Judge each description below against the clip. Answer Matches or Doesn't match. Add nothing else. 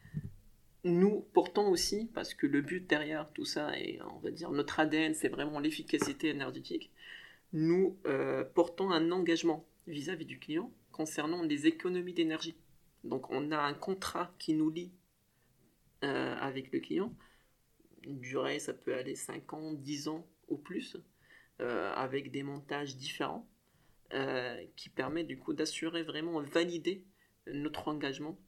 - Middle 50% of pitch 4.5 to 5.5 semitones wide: Doesn't match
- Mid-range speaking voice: Matches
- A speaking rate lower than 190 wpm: Matches